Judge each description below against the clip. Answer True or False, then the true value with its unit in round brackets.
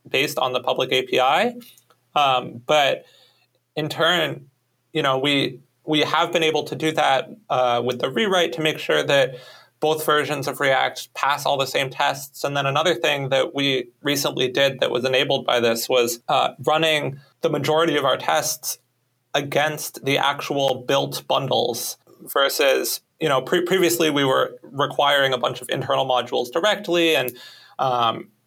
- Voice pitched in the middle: True (145 Hz)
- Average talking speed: True (165 wpm)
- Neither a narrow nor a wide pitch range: True (3.1 semitones)